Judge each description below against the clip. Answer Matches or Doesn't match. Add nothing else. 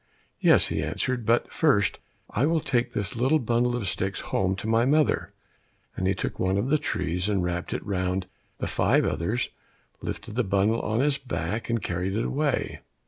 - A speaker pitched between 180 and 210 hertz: Doesn't match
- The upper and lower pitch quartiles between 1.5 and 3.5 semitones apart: Doesn't match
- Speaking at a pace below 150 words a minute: Doesn't match